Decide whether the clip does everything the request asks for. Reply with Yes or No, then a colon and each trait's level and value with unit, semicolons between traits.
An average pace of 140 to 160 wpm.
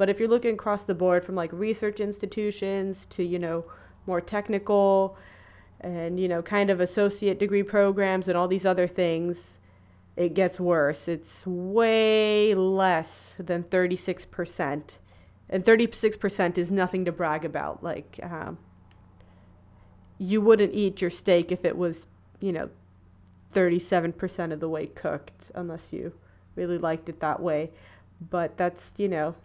Yes: average, 145 wpm